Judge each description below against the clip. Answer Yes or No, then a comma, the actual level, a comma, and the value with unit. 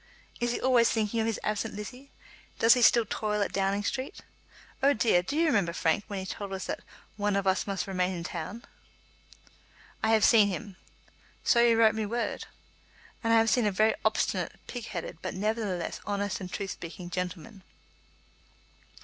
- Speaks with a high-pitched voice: Yes, high, 210 Hz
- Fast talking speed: No, average, 185 wpm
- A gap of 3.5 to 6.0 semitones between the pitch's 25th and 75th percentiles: No, average, 3.1 semitones